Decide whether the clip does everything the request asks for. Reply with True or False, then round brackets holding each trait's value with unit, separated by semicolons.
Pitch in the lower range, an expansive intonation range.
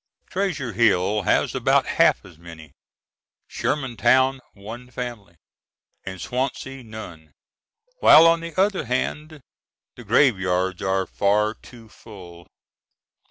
True (115 Hz; 5.8 semitones)